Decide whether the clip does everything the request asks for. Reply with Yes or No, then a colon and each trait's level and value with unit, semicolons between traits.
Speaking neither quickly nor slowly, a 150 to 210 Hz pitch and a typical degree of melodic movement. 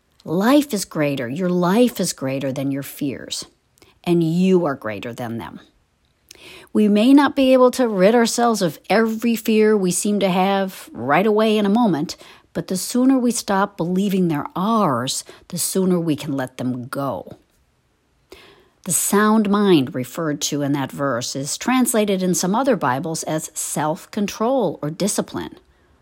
No: average, 160 wpm; medium, 185 Hz; wide, 6.7 semitones